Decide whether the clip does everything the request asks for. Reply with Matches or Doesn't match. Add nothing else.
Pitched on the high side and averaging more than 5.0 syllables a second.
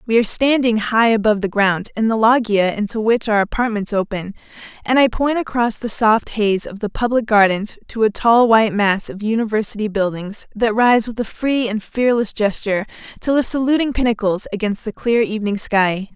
Matches